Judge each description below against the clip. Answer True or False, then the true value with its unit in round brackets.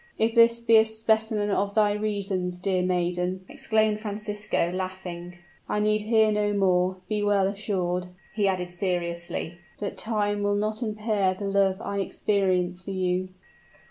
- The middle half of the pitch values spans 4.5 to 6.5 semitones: False (2.6 semitones)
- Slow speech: False (150 wpm)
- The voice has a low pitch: False (200 Hz)